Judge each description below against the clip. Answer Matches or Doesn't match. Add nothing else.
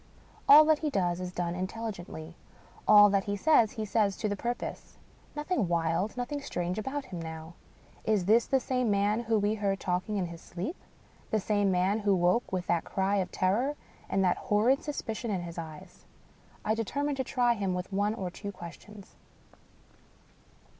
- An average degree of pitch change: Matches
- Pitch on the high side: Matches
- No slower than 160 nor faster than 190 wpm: Matches